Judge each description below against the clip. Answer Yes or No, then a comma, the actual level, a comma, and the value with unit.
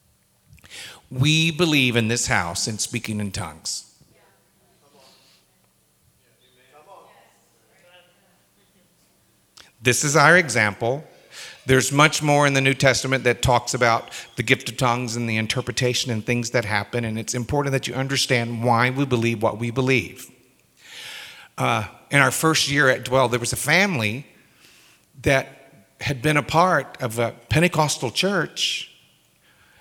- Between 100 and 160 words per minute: Yes, slow, 135 wpm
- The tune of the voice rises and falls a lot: No, average, 3.3 semitones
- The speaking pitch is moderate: No, low, 125 Hz